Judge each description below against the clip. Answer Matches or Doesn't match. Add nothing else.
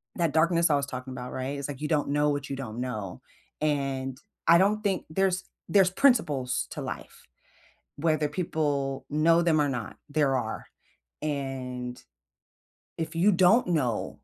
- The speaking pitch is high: Doesn't match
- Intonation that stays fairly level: Doesn't match